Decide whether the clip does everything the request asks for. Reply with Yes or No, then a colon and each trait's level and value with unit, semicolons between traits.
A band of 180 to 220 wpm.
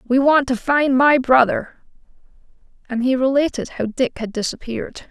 No: average, 155 wpm